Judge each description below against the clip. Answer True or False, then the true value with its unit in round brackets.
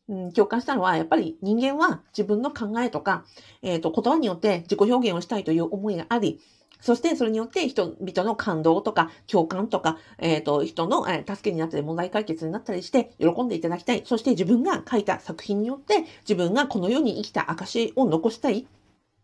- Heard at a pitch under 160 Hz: False (210 Hz)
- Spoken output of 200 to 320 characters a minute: False (400 characters per minute)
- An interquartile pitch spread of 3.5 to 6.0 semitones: True (5.4 semitones)